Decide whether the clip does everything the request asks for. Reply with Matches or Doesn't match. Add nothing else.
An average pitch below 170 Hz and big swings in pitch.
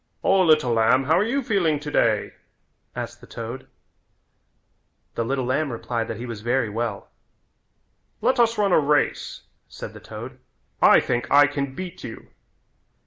Matches